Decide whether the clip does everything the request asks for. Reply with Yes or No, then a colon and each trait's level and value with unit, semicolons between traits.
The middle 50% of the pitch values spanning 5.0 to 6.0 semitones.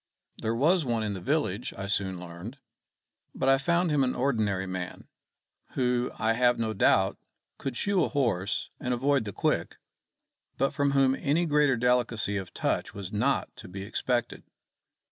Yes: average, 5.3 semitones